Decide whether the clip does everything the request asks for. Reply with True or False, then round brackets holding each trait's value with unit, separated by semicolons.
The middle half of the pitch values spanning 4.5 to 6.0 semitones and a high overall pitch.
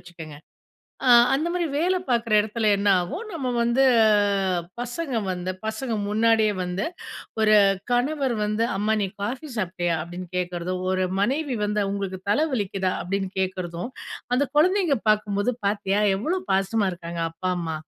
True (5.2 semitones; 210 Hz)